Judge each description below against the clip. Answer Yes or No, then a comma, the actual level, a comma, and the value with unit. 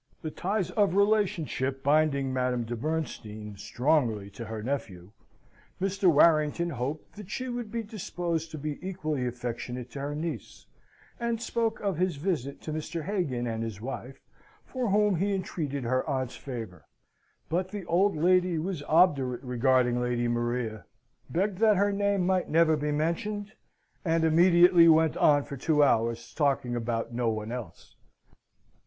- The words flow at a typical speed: Yes, average, 155 wpm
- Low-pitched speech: No, medium, 150 Hz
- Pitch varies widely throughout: Yes, wide, 6.9 semitones